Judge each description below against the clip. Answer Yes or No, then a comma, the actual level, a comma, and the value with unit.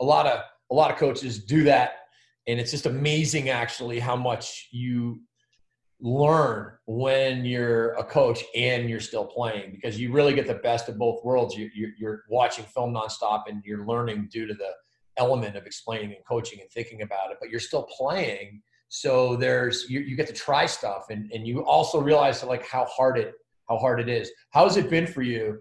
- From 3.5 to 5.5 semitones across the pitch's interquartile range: No, average, 3.0 semitones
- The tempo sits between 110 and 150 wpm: No, fast, 205 wpm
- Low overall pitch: Yes, low, 120 Hz